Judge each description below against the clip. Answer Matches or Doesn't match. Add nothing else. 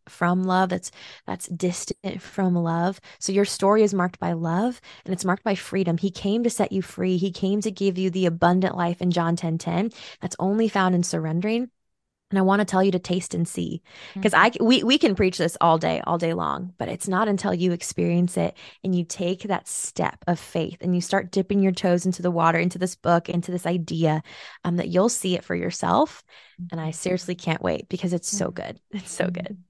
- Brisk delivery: Matches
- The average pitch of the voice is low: Doesn't match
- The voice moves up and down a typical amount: Doesn't match